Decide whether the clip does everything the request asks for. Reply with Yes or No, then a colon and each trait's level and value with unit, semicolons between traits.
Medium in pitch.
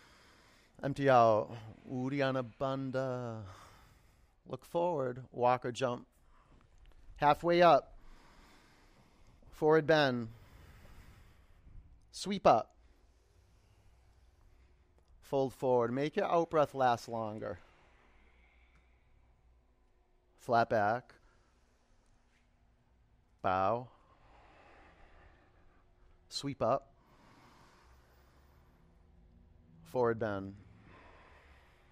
No: very low, 95 Hz